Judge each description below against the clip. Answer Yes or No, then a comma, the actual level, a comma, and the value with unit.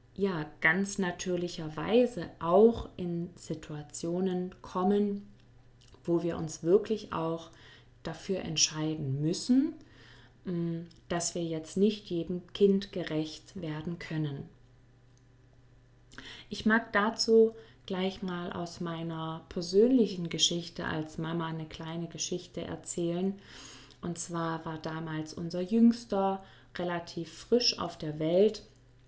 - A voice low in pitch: No, medium, 170 Hz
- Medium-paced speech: No, slow, 105 wpm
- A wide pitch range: No, average, 3.5 semitones